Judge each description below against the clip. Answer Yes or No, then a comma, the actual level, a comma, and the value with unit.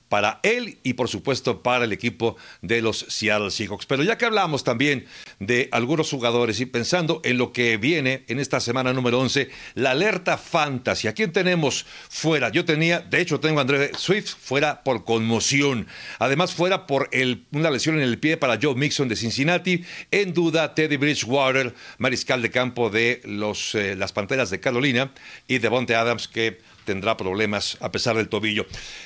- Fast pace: No, average, 180 wpm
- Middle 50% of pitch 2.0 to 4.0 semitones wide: No, average, 4.5 semitones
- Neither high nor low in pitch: No, low, 130 Hz